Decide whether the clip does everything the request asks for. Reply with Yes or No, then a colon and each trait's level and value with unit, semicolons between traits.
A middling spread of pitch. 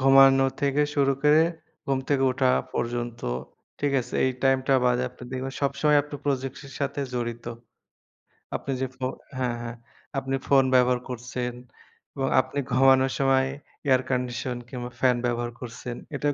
No: narrow, 1.8 semitones